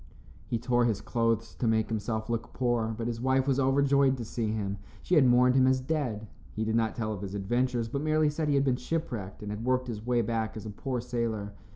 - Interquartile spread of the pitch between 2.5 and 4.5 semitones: Yes, average, 3.0 semitones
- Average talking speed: No, fast, 245 wpm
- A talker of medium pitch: No, low, 120 Hz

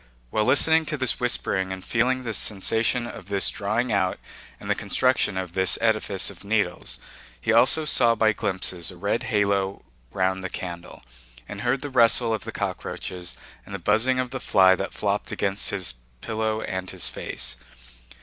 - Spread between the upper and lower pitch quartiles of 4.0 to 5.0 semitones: Yes, average, 4.3 semitones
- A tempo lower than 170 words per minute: No, average, 175 wpm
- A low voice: Yes, low, 105 Hz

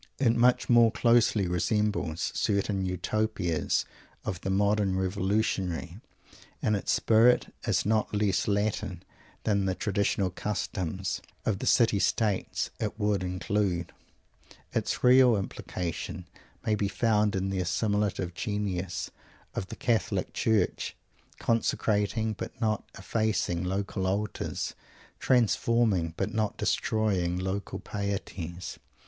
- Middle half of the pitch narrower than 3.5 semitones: Yes, average, 2.7 semitones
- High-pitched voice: No, low, 100 Hz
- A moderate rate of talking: No, slow, 115 wpm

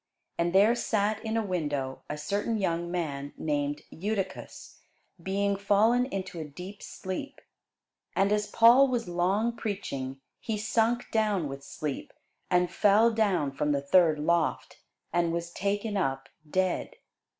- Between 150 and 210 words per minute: No, average, 140 wpm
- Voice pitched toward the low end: No, high, 190 Hz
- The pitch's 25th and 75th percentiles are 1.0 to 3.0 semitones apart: No, average, 5.1 semitones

